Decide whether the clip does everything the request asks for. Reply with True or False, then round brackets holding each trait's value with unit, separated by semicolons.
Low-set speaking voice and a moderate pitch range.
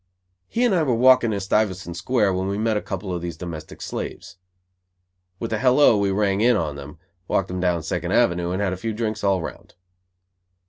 True (100 Hz; 4.1 semitones)